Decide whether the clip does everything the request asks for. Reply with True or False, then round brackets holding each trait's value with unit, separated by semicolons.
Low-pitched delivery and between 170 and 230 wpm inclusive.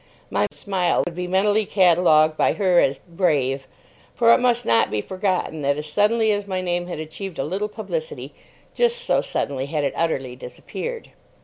False (180 Hz; 180 wpm)